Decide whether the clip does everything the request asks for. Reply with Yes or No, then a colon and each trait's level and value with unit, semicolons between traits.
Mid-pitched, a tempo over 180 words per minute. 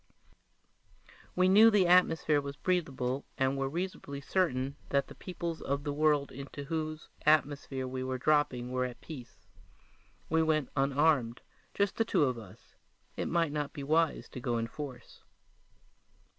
No: medium, 145 Hz; average, 160 wpm